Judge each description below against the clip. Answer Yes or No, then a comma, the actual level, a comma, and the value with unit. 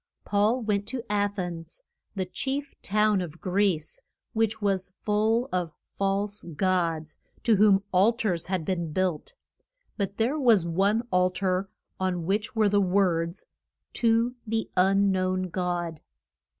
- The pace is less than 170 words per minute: Yes, average, 140 wpm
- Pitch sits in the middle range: No, high, 195 Hz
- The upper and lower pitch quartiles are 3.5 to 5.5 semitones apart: No, average, 2.8 semitones